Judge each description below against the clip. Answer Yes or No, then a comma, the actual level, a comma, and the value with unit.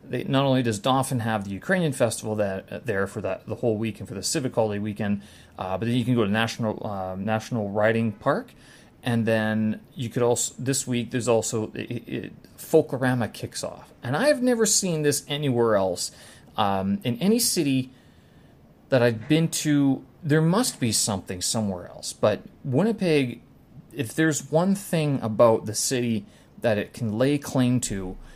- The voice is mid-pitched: No, low, 120 Hz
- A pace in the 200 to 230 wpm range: No, average, 175 wpm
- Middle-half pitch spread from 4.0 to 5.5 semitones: Yes, average, 4.7 semitones